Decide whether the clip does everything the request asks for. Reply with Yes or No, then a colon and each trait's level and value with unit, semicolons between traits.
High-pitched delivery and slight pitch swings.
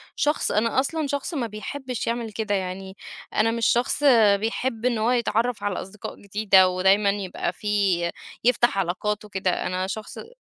No: high, 215 Hz; average, 3.7 semitones